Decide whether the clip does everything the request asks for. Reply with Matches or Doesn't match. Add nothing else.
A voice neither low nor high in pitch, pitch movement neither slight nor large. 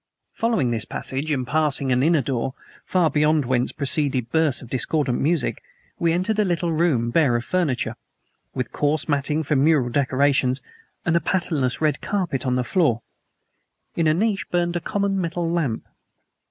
Matches